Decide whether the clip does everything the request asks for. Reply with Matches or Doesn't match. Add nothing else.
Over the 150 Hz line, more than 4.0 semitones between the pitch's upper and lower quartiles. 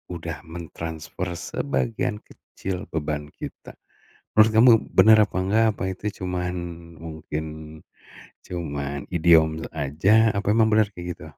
Doesn't match